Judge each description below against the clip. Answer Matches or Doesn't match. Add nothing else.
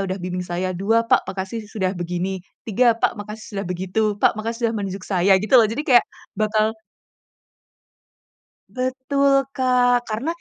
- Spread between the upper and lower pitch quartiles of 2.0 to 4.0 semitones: Doesn't match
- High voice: Matches